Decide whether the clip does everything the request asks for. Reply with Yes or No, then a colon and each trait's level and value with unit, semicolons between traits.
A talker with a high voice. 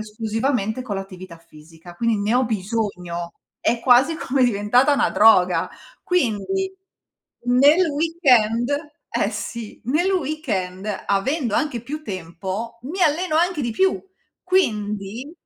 Yes: high, 235 Hz